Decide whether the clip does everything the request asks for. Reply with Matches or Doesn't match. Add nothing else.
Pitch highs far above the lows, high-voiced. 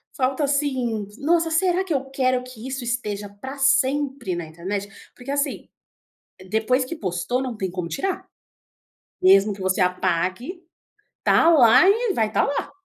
Matches